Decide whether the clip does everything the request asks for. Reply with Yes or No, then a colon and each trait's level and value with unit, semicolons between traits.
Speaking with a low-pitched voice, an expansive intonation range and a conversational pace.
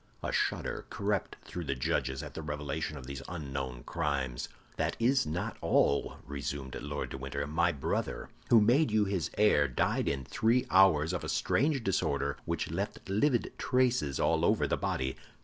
Yes: very low, 75 Hz; wide, 6.9 semitones; average, 170 wpm